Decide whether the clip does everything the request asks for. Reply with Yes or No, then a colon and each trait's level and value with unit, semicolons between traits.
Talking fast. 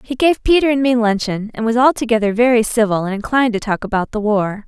Yes: fast, 230 wpm